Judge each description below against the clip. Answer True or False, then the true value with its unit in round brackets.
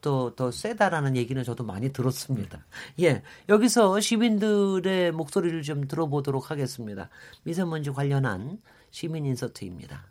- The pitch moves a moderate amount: False (6.3 semitones)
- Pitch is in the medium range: True (145 Hz)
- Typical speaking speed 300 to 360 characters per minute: True (335 characters per minute)